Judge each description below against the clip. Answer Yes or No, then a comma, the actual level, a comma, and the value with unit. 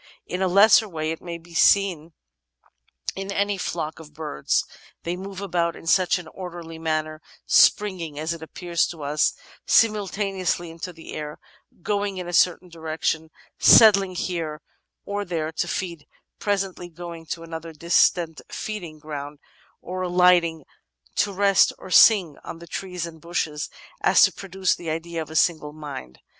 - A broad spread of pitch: No, average, 2.8 semitones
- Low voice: No, medium, 170 Hz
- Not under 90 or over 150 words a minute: No, average, 160 wpm